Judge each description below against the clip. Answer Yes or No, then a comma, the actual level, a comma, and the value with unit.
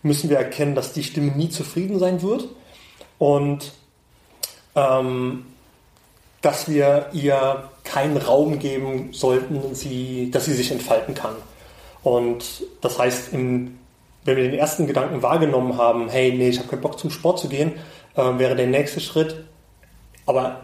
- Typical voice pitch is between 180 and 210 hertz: No, medium, 140 Hz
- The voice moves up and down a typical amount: Yes, average, 3.1 semitones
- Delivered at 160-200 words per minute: No, average, 150 wpm